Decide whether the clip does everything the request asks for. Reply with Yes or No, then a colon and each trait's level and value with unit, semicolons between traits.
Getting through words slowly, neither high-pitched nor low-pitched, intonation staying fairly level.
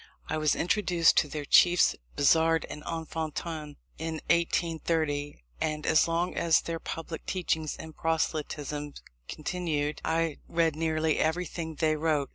Yes: slow, 130 wpm; medium, 160 Hz; narrow, 1.5 semitones